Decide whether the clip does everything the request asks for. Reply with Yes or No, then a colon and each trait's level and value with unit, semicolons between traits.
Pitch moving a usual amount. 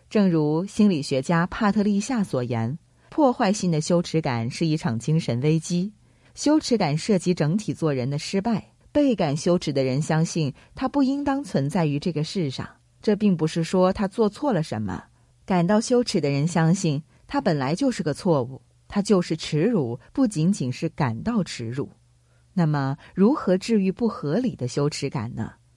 No: wide, 6.7 semitones